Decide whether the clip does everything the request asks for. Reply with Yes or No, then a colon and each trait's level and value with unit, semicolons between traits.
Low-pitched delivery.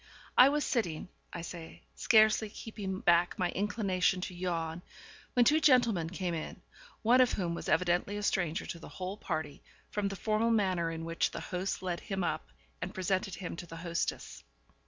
No: medium, 185 Hz